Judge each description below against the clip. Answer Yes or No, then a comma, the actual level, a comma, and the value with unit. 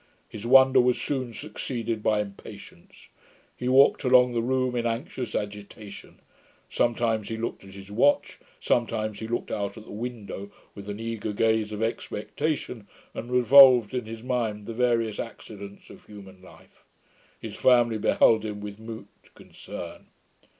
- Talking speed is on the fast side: No, average, 150 wpm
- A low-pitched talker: Yes, low, 115 Hz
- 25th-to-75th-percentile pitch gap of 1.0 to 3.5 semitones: Yes, average, 2.9 semitones